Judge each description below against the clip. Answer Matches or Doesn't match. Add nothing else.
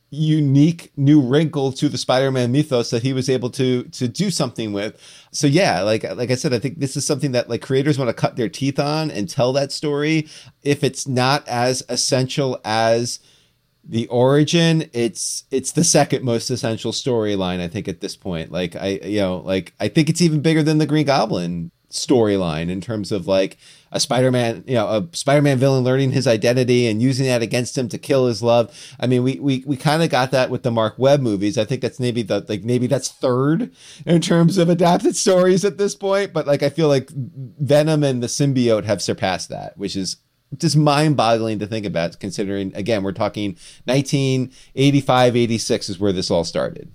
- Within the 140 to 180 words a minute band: Doesn't match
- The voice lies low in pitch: Matches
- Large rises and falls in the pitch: Doesn't match